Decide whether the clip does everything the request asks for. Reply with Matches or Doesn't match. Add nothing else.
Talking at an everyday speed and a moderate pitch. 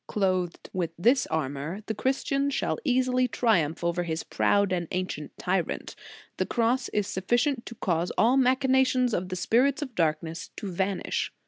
Doesn't match